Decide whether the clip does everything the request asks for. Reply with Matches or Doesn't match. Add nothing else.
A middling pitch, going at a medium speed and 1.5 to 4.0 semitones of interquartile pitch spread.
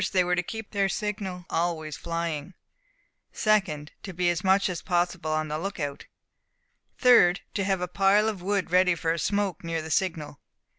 Matches